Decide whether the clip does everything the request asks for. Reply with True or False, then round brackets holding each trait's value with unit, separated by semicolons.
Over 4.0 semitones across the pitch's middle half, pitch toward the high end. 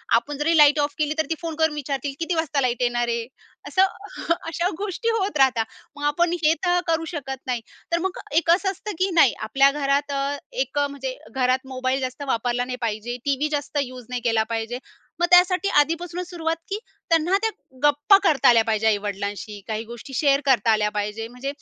True (5.2 semitones; 275 Hz)